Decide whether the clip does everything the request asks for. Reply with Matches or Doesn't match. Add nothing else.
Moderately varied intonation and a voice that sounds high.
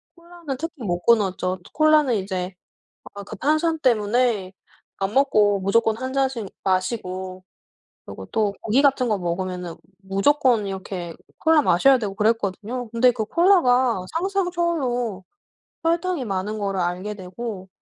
Doesn't match